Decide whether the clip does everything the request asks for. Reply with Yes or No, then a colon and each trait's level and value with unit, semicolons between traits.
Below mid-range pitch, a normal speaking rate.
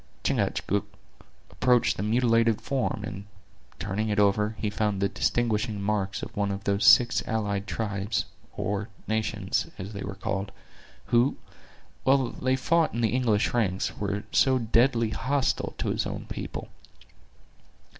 Yes: low, 105 Hz; average, 145 wpm